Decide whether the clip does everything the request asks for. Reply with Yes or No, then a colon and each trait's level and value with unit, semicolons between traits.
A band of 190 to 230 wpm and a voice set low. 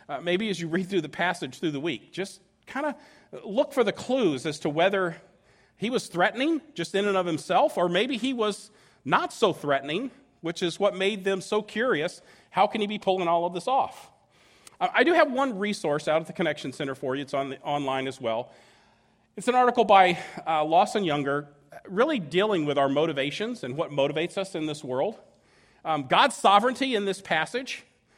No: fast, 205 wpm; medium, 185 Hz